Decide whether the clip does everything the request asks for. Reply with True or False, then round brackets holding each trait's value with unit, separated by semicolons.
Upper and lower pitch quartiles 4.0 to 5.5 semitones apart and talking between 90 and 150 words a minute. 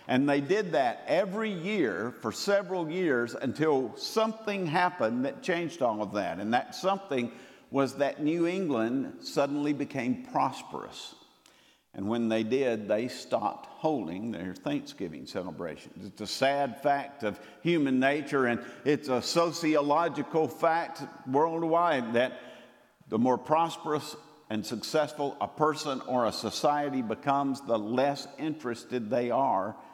True (4.6 semitones; 135 wpm)